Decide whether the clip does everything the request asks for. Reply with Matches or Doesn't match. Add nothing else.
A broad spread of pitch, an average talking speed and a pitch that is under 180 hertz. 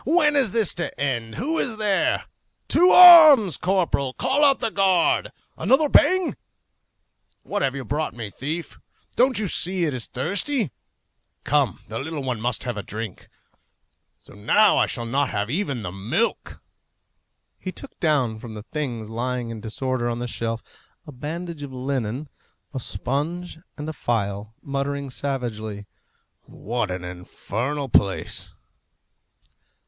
Matches